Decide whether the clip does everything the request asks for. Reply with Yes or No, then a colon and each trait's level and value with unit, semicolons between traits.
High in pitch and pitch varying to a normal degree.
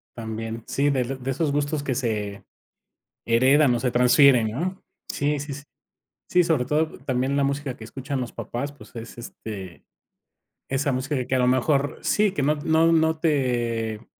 No: low, 135 Hz; average, 3.3 semitones